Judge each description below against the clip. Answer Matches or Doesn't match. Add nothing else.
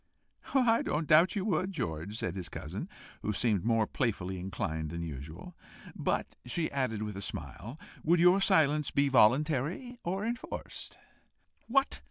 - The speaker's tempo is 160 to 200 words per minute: Doesn't match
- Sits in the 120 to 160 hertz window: Matches